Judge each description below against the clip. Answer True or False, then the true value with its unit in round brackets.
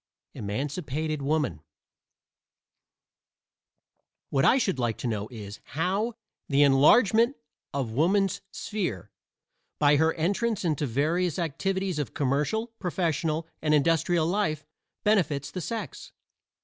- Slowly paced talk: True (110 wpm)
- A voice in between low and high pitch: True (160 Hz)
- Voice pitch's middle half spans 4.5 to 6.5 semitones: True (5.3 semitones)